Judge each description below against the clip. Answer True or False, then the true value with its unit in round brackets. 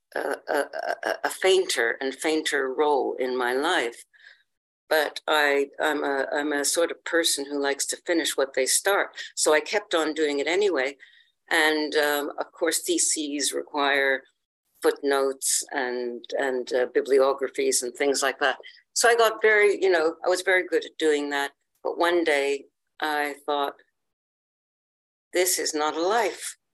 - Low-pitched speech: False (150 Hz)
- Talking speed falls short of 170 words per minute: True (160 wpm)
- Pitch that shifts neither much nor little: True (4.0 semitones)